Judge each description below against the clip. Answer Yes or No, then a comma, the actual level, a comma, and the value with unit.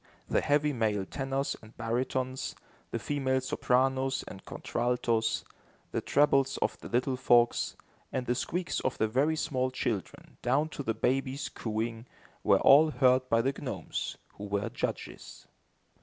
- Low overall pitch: Yes, low, 130 Hz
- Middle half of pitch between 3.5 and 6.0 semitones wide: No, average, 2.7 semitones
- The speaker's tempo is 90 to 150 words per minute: Yes, average, 145 wpm